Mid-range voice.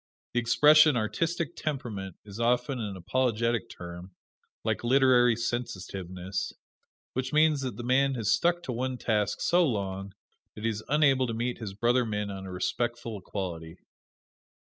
No: low, 120 Hz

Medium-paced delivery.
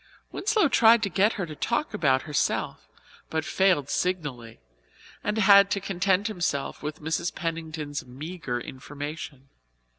No: slow, 130 wpm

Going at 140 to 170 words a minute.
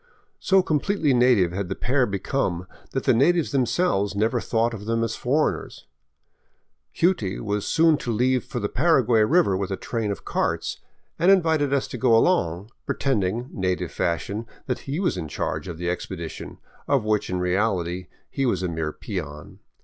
No: average, 180 wpm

